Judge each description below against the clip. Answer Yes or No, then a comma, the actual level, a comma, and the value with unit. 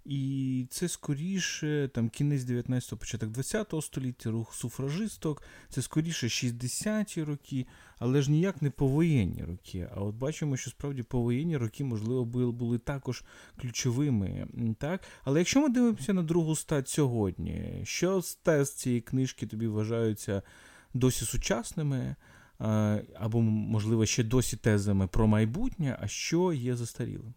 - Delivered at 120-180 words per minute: Yes, average, 135 wpm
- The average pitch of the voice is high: No, low, 130 Hz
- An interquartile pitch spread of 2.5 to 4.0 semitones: No, average, 4.5 semitones